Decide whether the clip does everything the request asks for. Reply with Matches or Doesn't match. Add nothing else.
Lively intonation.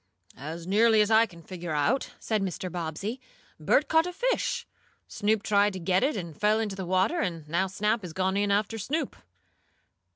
Doesn't match